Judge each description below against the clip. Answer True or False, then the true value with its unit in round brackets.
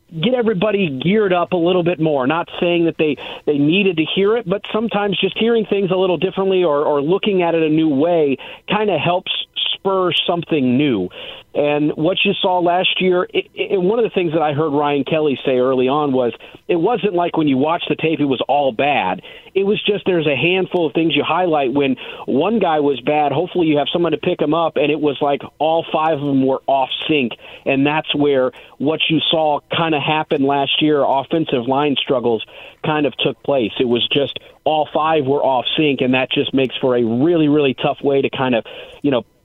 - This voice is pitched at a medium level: True (160 Hz)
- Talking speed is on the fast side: True (220 wpm)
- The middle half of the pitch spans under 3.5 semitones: False (4.2 semitones)